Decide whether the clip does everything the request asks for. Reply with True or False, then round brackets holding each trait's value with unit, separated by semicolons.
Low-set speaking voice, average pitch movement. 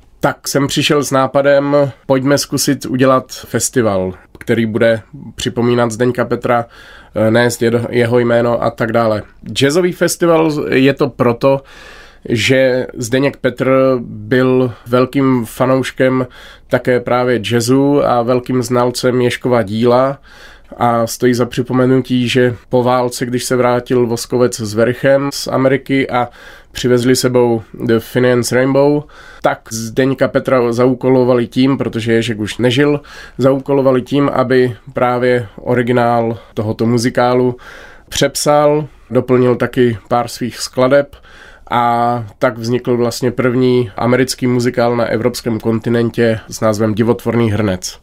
False (125 Hz; 1.9 semitones)